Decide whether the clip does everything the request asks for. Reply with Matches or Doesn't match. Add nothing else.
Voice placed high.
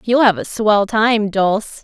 Matches